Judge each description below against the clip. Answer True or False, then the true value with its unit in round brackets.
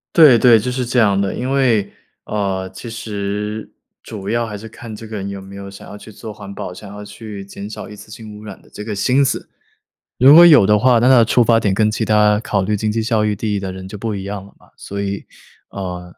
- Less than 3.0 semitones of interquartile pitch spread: True (2.5 semitones)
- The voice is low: True (105 Hz)